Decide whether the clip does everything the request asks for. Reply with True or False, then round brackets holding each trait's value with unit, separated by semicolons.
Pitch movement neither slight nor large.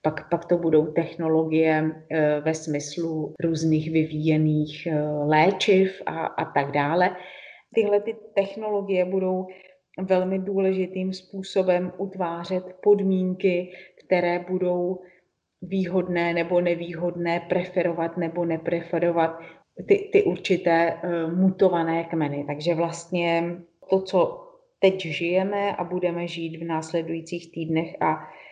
False (2.3 semitones)